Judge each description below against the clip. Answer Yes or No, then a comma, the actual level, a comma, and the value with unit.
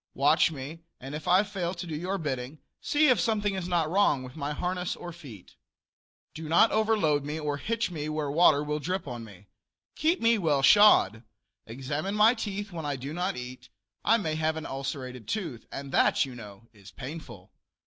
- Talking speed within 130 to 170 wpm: No, average, 195 wpm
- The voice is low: No, medium, 155 Hz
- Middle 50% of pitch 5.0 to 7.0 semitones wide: Yes, wide, 5.6 semitones